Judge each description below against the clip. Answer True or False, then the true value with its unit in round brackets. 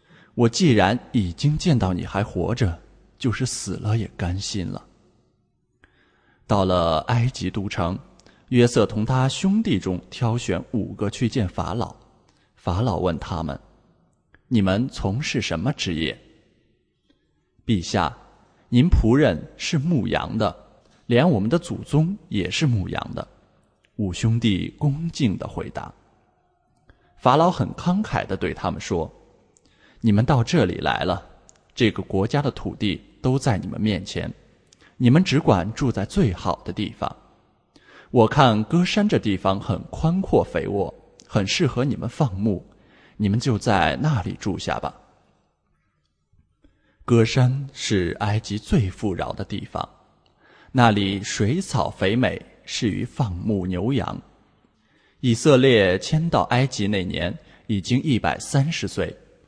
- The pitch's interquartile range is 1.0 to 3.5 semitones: False (5.2 semitones)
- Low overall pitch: True (115 Hz)